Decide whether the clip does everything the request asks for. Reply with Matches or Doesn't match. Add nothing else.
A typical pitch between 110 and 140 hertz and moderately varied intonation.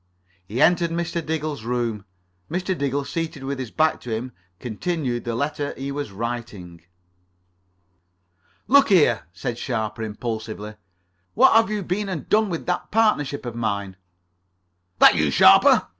Doesn't match